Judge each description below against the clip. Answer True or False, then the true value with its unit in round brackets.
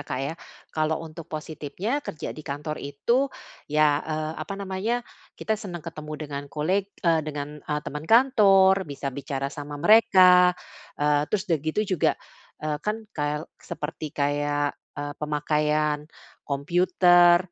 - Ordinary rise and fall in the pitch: True (3.6 semitones)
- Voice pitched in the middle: True (155 Hz)